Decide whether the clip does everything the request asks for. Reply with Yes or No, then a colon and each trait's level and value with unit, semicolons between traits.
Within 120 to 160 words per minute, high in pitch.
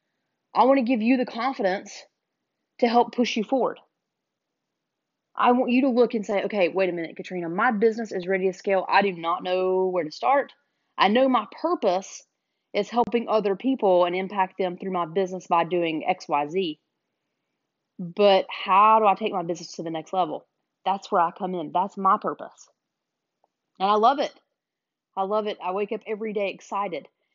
No: average, 195 wpm; high, 195 Hz